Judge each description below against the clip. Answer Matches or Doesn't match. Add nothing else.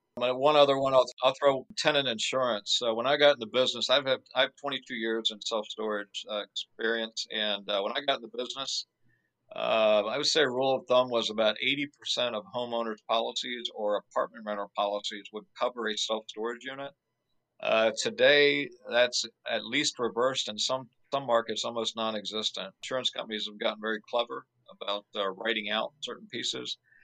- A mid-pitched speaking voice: Doesn't match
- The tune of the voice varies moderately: Matches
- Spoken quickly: Doesn't match